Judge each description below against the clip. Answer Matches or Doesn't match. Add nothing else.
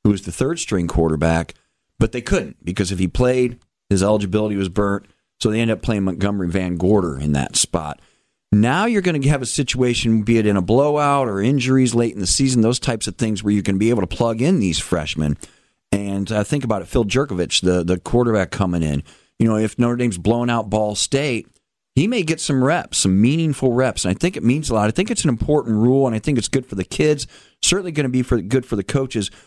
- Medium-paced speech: Doesn't match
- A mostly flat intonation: Doesn't match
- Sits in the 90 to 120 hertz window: Matches